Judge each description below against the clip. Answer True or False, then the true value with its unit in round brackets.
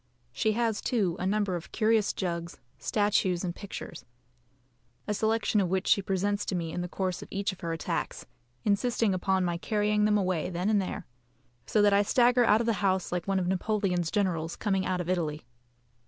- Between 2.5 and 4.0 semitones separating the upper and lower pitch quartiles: True (2.9 semitones)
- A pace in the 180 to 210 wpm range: True (200 wpm)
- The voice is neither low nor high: False (195 Hz)